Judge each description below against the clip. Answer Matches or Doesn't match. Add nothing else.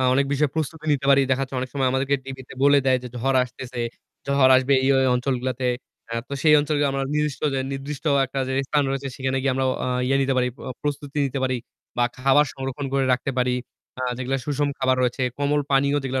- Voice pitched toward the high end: Doesn't match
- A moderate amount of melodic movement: Doesn't match